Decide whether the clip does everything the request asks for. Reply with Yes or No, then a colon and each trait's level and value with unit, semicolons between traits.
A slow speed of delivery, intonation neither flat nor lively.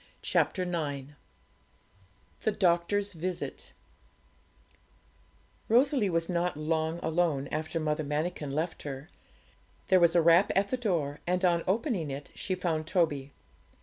Yes: slow, 125 wpm; average, 3.2 semitones